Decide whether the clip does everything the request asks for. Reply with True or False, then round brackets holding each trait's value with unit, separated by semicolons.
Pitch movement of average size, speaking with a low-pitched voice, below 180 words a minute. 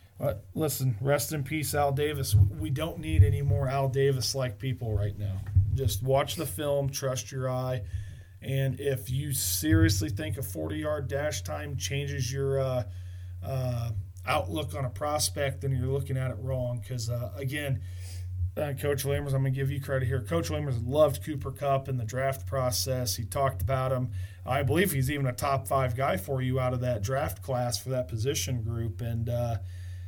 False (4.9 semitones; 125 Hz; 185 wpm)